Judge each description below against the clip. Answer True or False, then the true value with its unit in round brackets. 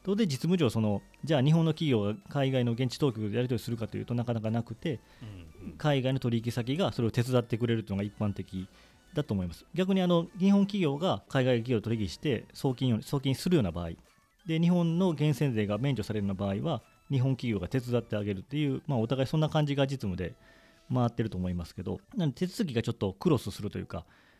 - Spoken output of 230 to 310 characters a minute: False (440 characters per minute)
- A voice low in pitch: True (120 Hz)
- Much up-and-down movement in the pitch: True (6.0 semitones)